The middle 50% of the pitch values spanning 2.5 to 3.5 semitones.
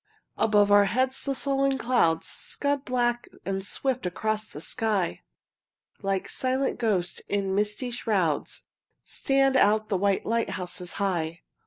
No: average, 4.9 semitones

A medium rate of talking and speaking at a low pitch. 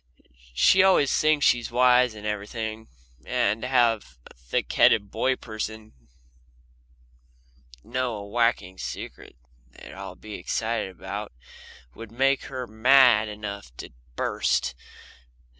No: slow, 125 wpm; low, 110 Hz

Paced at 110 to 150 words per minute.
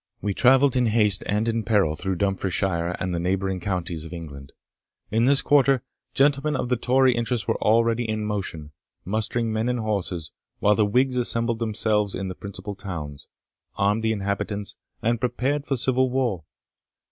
No: average, 170 wpm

